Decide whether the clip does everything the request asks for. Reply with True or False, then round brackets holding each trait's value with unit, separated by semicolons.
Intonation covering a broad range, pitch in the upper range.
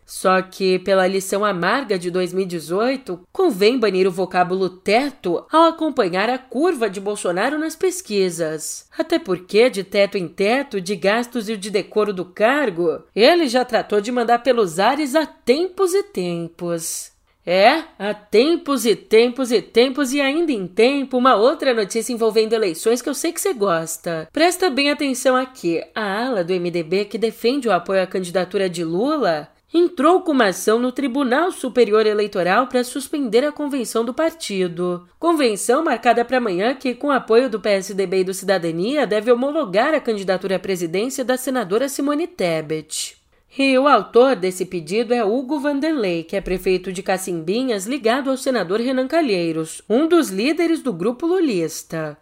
True (6.3 semitones; 225 Hz)